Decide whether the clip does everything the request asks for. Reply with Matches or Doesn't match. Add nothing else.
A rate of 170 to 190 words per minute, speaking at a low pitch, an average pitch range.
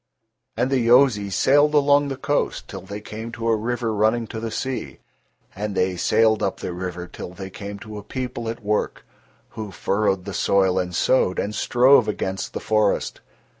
Matches